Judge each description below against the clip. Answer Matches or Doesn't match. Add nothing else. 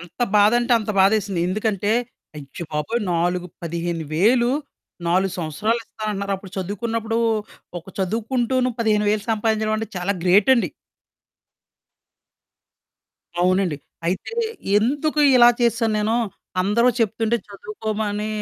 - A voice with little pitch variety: Doesn't match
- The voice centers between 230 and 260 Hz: Doesn't match